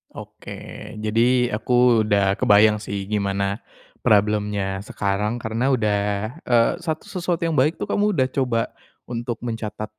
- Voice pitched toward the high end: No, low, 110 Hz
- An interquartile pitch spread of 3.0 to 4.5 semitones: Yes, average, 3.3 semitones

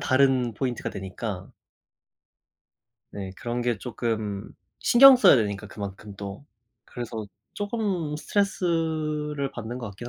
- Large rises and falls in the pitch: Yes, wide, 6.6 semitones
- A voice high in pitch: No, low, 125 Hz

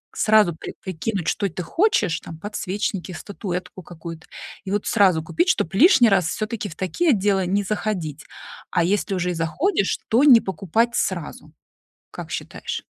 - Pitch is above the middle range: Yes, high, 195 Hz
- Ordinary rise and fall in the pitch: Yes, average, 3.7 semitones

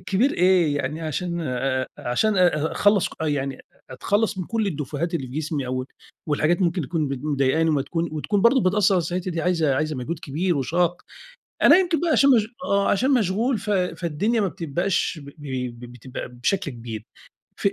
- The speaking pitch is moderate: Yes, medium, 165 Hz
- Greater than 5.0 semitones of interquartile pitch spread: Yes, wide, 5.4 semitones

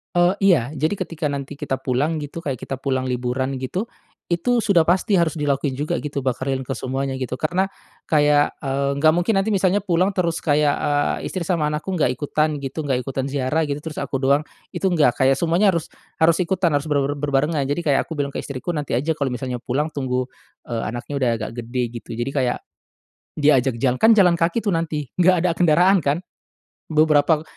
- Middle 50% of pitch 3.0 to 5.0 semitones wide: Yes, average, 3.9 semitones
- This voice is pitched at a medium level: Yes, medium, 145 Hz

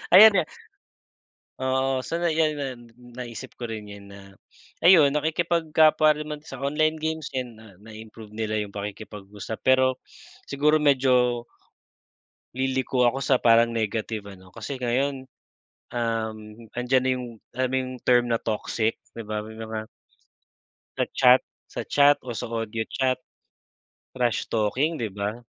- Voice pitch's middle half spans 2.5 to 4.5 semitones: Yes, average, 4.1 semitones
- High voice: No, low, 125 Hz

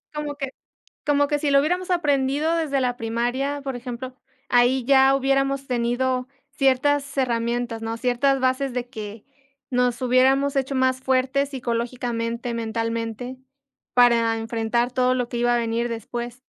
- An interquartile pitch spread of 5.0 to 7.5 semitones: No, narrow, 2.4 semitones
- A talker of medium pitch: No, very high, 255 Hz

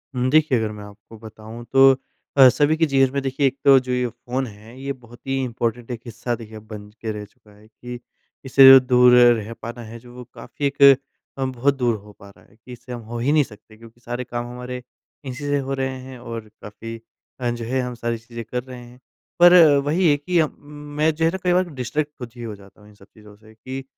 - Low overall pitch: Yes, low, 125 Hz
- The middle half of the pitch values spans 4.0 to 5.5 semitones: No, average, 3.0 semitones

